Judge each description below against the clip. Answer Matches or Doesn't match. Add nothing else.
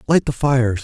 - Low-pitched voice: Matches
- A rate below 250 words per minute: Matches